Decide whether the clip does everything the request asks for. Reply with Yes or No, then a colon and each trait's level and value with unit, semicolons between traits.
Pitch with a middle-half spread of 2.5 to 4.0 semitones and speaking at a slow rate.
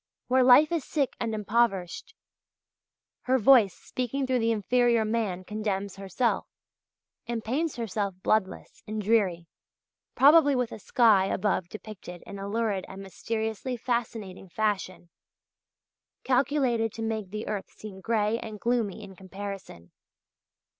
Yes: average, 3.5 semitones; slow, 130 wpm